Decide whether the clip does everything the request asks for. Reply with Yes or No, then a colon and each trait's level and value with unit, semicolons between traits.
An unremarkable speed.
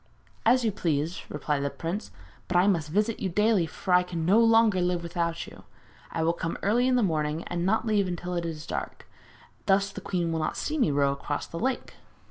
No: fast, 220 wpm